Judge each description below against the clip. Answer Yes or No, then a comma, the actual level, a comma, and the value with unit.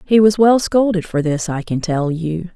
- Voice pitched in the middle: Yes, medium, 180 Hz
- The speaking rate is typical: No, fast, 235 wpm